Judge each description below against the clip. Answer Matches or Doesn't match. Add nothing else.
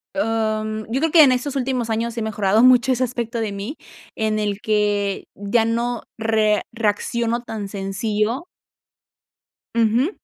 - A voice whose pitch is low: Doesn't match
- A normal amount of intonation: Doesn't match